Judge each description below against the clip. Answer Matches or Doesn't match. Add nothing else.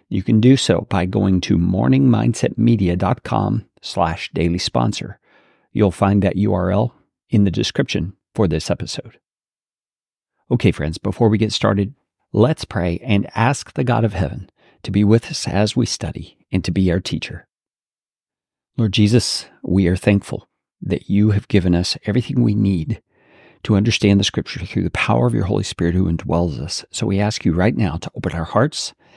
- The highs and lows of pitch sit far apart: Doesn't match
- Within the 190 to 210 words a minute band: Doesn't match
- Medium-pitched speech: Doesn't match